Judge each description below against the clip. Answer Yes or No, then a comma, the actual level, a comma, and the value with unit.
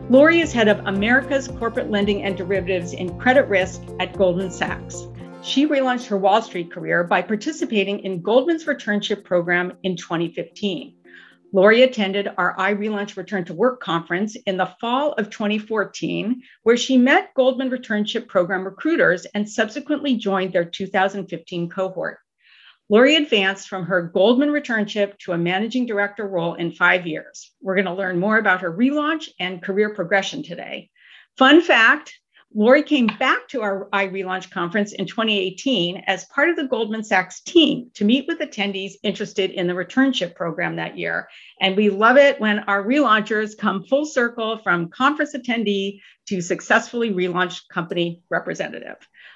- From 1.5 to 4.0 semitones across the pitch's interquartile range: No, average, 4.9 semitones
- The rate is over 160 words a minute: No, average, 155 wpm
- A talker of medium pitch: No, high, 205 Hz